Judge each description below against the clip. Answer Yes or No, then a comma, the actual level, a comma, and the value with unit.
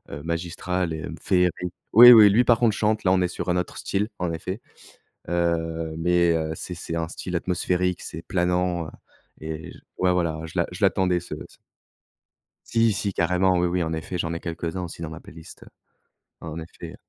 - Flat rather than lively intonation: Yes, narrow, 1.9 semitones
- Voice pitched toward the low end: Yes, very low, 90 Hz